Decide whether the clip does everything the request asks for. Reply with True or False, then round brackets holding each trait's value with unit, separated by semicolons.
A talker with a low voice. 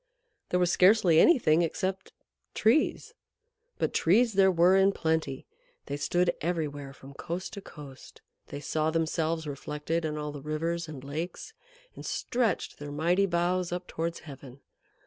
False (165 Hz)